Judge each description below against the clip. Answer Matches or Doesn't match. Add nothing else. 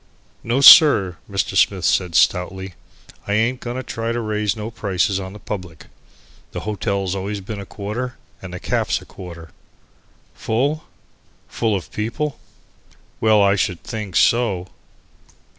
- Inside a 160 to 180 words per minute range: Doesn't match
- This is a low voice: Matches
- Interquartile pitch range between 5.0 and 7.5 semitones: Doesn't match